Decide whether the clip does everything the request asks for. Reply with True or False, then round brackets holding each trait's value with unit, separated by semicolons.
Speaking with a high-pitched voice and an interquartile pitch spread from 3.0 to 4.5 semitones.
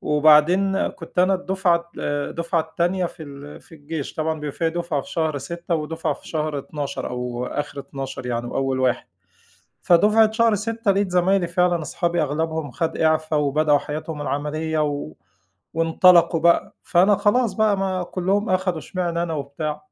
False (160 Hz; 3.6 semitones)